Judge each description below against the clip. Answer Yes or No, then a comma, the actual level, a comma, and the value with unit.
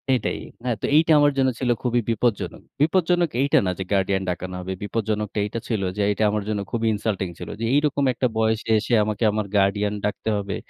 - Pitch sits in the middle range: No, low, 110 Hz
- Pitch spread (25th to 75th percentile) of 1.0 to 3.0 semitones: No, average, 3.5 semitones